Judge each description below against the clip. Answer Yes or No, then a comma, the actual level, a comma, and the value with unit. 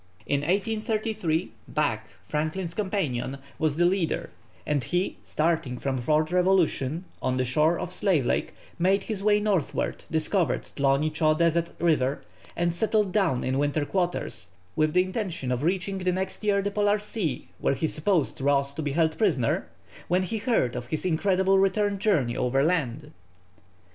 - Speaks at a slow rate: No, average, 160 wpm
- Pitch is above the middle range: No, medium, 165 Hz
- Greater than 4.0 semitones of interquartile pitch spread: Yes, average, 5.2 semitones